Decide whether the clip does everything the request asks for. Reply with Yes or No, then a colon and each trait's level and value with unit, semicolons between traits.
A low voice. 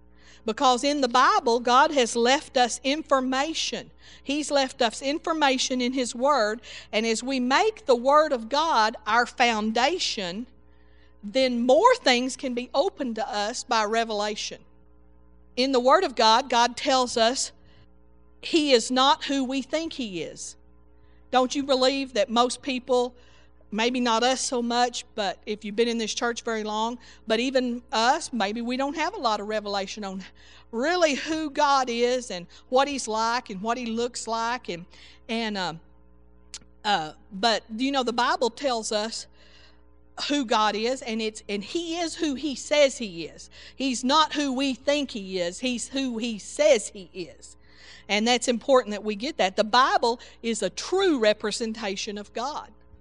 No: high, 240 Hz